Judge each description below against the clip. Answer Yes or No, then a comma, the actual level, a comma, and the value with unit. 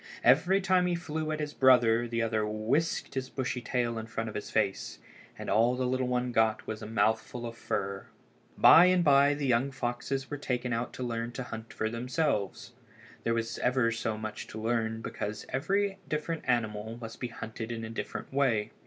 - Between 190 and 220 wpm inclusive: Yes, average, 195 wpm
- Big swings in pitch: No, average, 3.5 semitones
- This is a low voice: Yes, low, 120 Hz